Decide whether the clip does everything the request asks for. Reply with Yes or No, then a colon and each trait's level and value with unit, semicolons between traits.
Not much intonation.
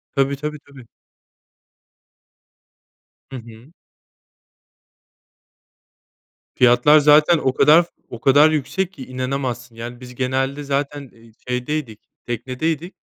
No: average, 3.2 semitones